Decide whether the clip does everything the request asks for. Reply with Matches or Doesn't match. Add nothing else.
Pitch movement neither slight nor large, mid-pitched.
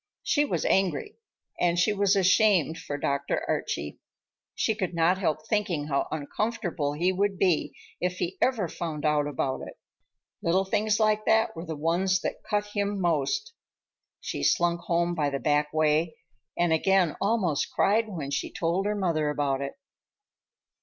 Matches